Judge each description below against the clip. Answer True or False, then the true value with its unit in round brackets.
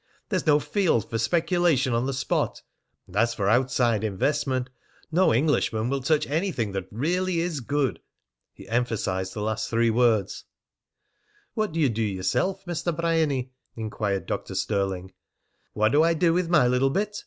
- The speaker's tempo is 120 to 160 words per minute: True (155 wpm)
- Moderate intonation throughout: False (6.9 semitones)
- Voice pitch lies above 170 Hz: False (130 Hz)